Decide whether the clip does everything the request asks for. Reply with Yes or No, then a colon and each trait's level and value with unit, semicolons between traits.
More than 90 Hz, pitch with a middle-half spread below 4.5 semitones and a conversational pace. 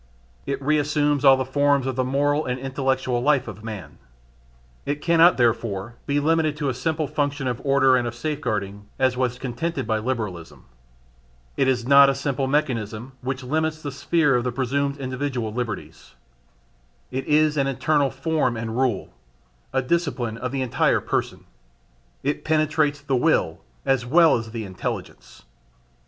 Yes: low, 135 Hz; average, 3.0 semitones; average, 160 wpm